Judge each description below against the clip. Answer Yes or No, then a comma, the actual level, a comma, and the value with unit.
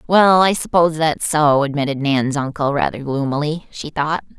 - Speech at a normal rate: Yes, average, 165 wpm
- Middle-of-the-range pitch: Yes, medium, 150 Hz